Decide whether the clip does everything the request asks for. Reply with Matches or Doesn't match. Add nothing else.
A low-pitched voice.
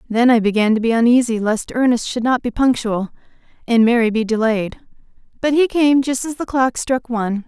Doesn't match